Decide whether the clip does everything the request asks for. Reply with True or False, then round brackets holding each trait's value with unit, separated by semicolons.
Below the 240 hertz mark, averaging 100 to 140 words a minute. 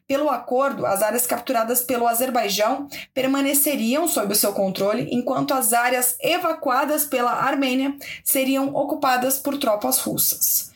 False (265 Hz; 130 wpm)